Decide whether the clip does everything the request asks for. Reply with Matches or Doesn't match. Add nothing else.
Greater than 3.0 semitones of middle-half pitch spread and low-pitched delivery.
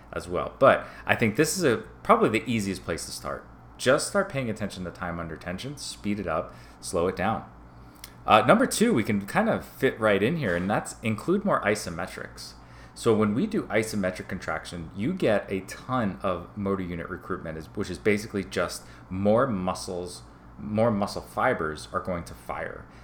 Matches